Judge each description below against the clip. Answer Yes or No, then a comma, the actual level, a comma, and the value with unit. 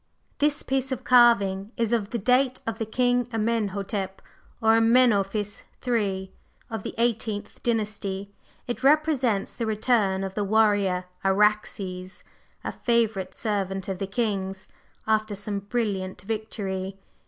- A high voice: Yes, high, 210 Hz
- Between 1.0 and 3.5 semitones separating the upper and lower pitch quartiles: Yes, average, 3.2 semitones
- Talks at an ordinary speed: No, slow, 130 wpm